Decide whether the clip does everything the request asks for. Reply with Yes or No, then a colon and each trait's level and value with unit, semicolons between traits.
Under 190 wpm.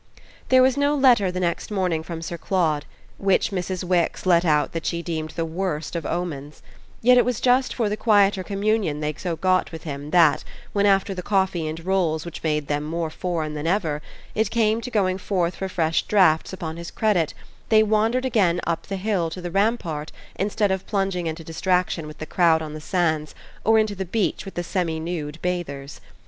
No: fast, 205 wpm